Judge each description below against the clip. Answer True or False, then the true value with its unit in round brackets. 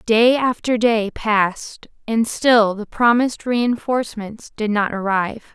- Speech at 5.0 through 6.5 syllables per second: False (4.2 syllables/s)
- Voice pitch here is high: True (225 Hz)